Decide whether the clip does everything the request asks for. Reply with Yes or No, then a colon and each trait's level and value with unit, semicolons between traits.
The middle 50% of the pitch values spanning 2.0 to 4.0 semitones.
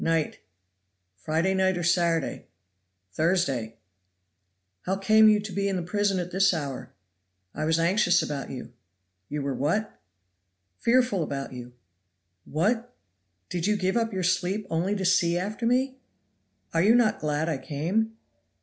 No: average, 4.7 semitones